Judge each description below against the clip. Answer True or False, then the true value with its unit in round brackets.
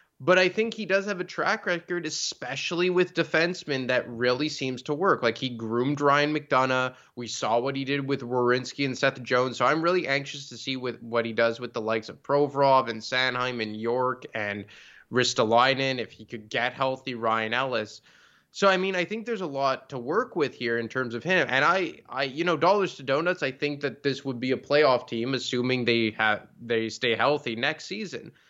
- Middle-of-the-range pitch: False (130 Hz)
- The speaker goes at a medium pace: False (210 wpm)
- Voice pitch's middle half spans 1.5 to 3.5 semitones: False (3.9 semitones)